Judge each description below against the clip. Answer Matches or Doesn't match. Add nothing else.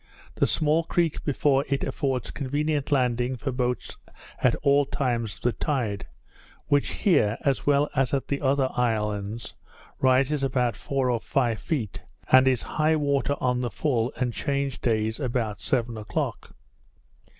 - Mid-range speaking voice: Doesn't match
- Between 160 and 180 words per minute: Doesn't match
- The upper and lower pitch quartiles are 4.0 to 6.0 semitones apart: Doesn't match